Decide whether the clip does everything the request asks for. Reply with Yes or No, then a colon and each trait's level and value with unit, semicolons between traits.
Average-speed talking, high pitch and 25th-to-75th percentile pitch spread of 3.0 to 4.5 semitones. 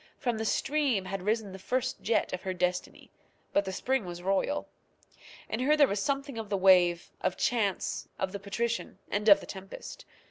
Yes: average, 190 wpm; high, 205 Hz; average, 4.2 semitones